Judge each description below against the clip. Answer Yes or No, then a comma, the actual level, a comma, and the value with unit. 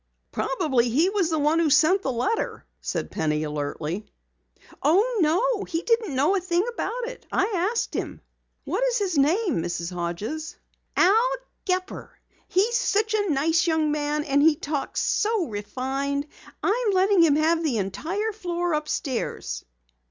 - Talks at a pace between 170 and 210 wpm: No, average, 150 wpm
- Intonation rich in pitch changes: Yes, wide, 6.5 semitones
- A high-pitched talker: Yes, very high, 325 Hz